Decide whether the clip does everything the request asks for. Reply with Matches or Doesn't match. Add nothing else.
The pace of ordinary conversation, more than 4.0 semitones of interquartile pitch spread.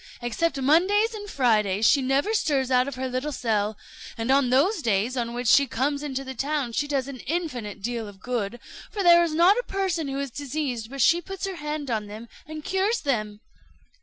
Doesn't match